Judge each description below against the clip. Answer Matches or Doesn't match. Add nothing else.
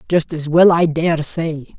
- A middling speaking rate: Matches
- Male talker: Doesn't match